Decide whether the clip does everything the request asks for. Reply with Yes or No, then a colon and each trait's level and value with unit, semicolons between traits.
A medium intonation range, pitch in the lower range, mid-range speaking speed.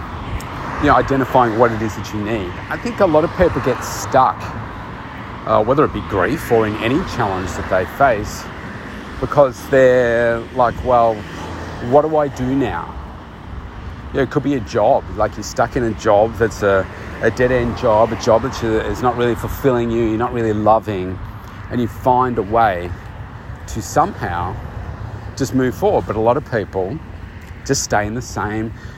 Yes: average, 3.5 semitones; low, 115 Hz; average, 180 wpm